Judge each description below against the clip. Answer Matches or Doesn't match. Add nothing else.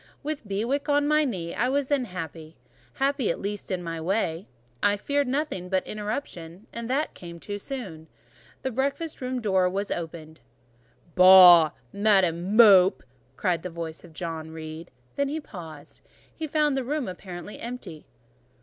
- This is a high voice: Matches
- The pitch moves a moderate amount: Doesn't match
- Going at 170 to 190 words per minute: Doesn't match